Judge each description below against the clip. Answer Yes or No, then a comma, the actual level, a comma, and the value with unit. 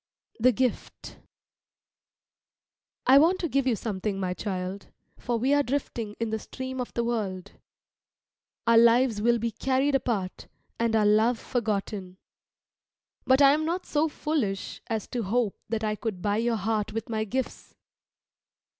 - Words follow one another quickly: No, average, 155 wpm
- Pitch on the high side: Yes, high, 230 Hz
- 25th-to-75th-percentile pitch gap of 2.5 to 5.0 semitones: Yes, average, 3.8 semitones